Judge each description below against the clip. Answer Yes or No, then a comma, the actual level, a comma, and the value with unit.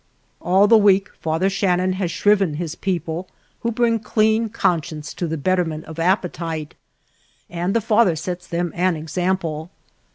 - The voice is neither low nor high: Yes, medium, 180 Hz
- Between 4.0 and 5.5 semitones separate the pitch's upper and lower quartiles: No, average, 3.3 semitones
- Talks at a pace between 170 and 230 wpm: No, average, 150 wpm